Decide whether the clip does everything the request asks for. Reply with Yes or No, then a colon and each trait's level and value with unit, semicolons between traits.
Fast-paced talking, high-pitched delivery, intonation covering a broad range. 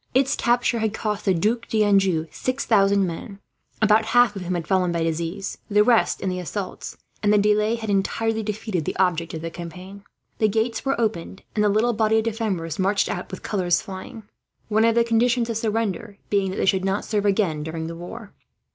No: fast, 210 wpm; high, 205 Hz; average, 3.3 semitones